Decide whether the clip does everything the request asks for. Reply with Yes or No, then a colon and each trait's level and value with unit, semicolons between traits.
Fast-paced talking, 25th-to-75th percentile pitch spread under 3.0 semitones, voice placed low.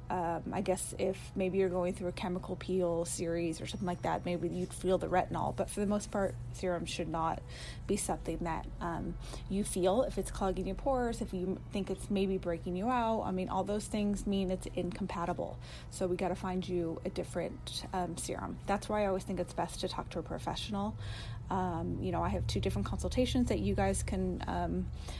No: fast, 215 wpm; narrow, 2.6 semitones; medium, 180 Hz